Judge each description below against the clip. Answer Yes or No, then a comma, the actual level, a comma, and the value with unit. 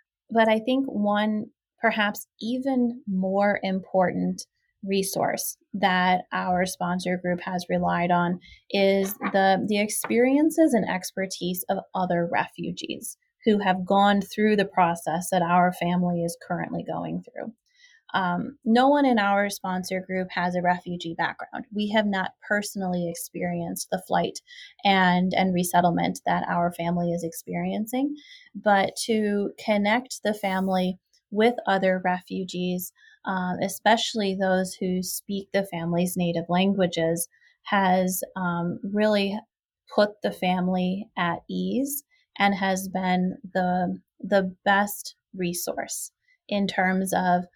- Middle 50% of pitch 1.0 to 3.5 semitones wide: Yes, average, 2.8 semitones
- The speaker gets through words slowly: Yes, slow, 125 wpm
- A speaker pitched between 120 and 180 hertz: No, high, 190 Hz